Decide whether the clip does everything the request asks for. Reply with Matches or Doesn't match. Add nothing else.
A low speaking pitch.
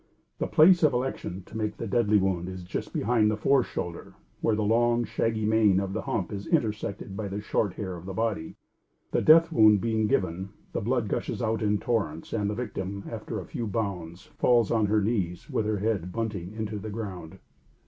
Matches